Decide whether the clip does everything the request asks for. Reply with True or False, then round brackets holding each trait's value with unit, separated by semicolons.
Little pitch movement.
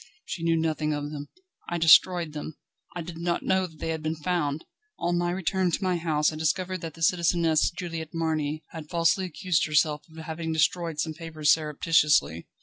True (2.0 semitones)